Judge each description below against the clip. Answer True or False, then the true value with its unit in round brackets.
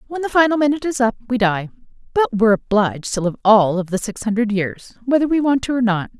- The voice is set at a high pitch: True (235 Hz)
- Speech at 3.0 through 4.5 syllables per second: False (6.4 syllables/s)